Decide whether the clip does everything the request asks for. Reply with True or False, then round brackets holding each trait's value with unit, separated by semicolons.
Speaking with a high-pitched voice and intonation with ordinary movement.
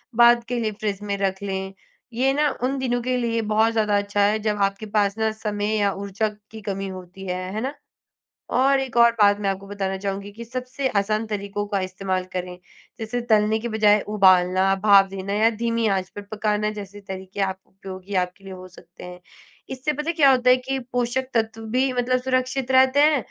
True (210 Hz; 3.7 semitones)